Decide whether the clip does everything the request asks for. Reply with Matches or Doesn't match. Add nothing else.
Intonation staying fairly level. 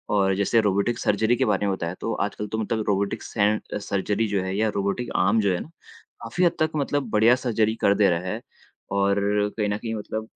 Matches